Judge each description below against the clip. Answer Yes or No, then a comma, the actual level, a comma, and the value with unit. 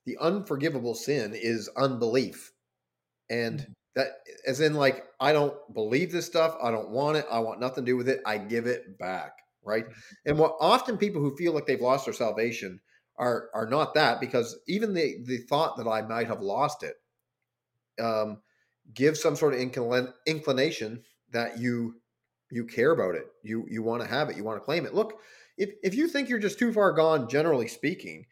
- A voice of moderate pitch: No, low, 125 Hz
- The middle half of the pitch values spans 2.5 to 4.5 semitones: No, wide, 5.5 semitones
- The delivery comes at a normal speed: Yes, average, 195 wpm